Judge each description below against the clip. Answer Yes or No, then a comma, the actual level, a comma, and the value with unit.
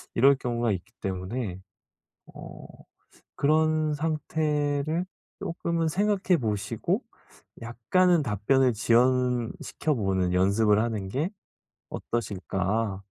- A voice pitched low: Yes, low, 120 Hz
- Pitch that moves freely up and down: Yes, wide, 6.9 semitones